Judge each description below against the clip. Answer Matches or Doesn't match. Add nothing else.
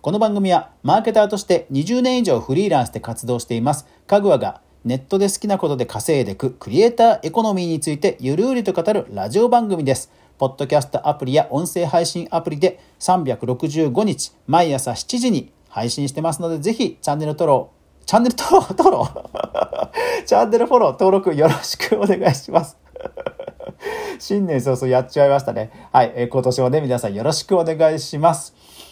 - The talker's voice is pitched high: Doesn't match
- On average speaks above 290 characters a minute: Matches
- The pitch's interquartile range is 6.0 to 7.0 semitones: Doesn't match